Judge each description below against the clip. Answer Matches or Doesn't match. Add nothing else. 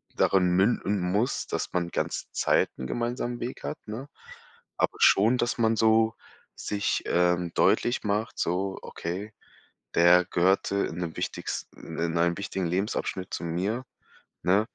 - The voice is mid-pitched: Doesn't match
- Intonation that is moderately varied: Matches